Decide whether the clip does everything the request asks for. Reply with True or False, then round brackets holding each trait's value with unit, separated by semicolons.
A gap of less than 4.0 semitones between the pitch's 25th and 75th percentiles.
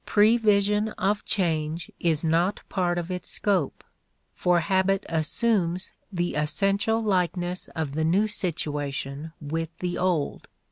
True (3.6 semitones)